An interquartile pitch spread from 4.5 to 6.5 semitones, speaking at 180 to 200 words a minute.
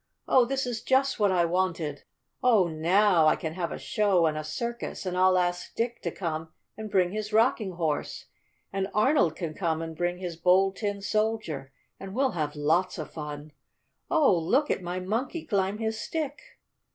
Yes: average, 4.8 semitones; average, 185 wpm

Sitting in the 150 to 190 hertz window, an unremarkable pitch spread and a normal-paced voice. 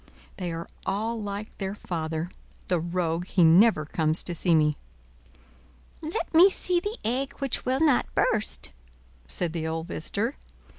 No: medium, 185 Hz; wide, 6.5 semitones; average, 150 wpm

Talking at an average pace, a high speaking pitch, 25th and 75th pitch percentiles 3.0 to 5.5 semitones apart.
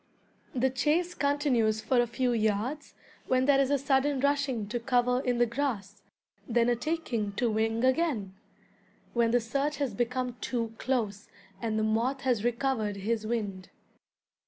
Yes: average, 160 wpm; high, 245 Hz; average, 3.4 semitones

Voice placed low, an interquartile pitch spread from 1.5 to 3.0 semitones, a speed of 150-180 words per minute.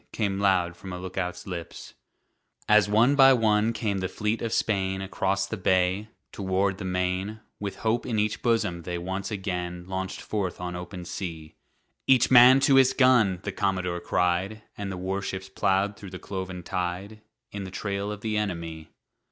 Yes: very low, 95 Hz; average, 2.7 semitones; average, 175 wpm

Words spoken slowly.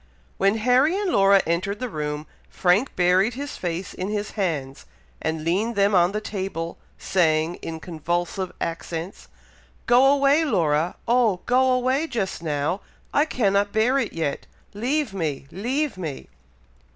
No: average, 145 wpm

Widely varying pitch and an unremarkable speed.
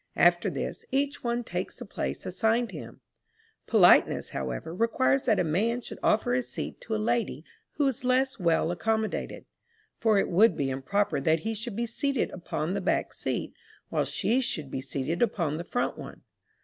Yes: wide, 6.1 semitones; average, 180 wpm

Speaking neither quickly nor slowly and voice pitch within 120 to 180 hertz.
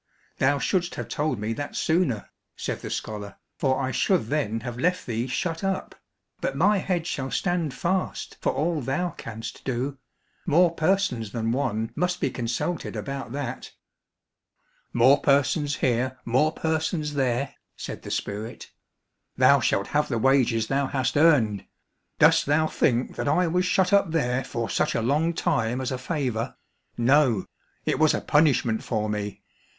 Yes: average, 160 wpm; low, 135 Hz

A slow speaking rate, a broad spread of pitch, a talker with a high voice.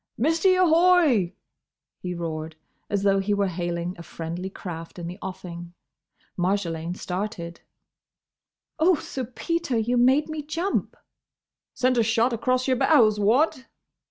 Yes: slow, 130 wpm; wide, 7.2 semitones; high, 210 Hz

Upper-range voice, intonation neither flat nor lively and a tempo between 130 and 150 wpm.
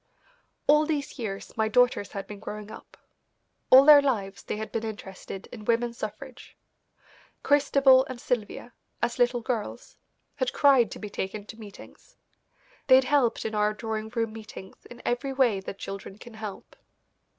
No: high, 230 Hz; average, 3.5 semitones; average, 160 wpm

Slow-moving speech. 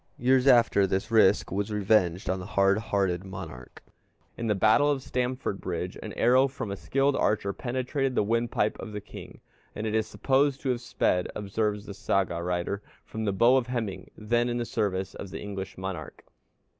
No: average, 185 wpm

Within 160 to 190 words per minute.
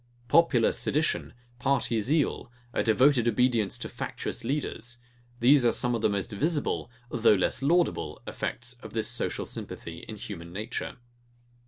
No: average, 145 wpm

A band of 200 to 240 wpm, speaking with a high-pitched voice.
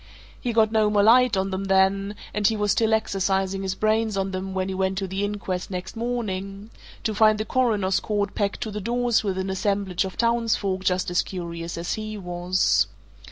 Yes: fast, 205 wpm; high, 195 Hz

